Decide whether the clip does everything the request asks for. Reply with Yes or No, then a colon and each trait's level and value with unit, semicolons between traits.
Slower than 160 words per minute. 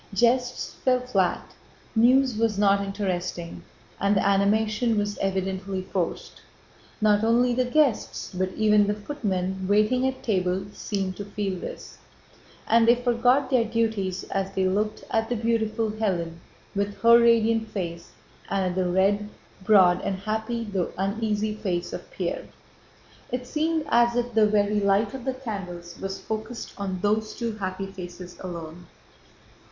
Yes: average, 150 wpm